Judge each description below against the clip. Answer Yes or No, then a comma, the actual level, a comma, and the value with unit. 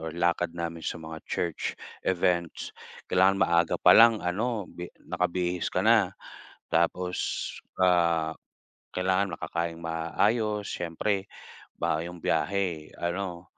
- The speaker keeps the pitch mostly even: Yes, narrow, 2.0 semitones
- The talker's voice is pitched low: Yes, very low, 85 Hz